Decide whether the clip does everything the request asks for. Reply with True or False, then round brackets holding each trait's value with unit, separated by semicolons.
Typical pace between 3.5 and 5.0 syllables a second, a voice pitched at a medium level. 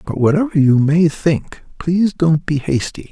True (4.6 syllables/s; 160 Hz)